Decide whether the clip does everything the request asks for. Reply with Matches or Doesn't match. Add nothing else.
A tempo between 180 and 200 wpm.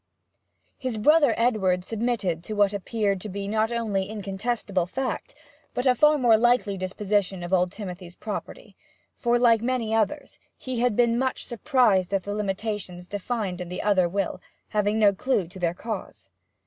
Doesn't match